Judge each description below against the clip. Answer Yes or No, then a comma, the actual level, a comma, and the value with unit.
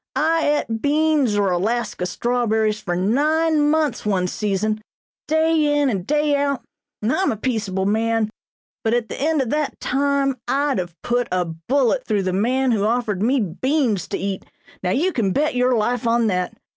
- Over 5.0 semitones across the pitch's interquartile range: Yes, wide, 5.6 semitones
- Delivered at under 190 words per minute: Yes, average, 180 wpm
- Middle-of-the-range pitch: No, high, 240 Hz